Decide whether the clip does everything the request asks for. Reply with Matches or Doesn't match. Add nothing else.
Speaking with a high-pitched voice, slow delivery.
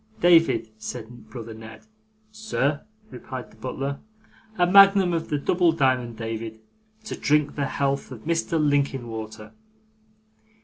Doesn't match